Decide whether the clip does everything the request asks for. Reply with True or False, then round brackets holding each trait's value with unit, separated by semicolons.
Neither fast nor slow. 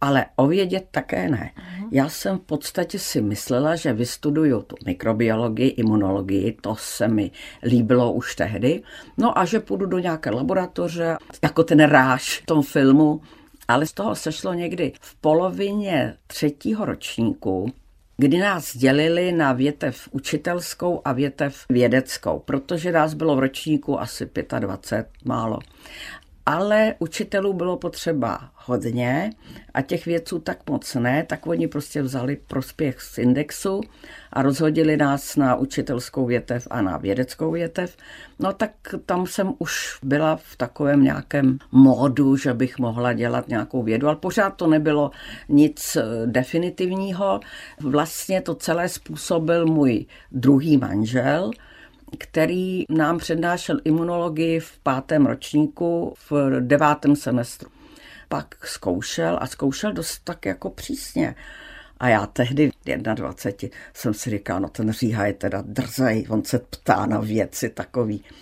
True (135 wpm)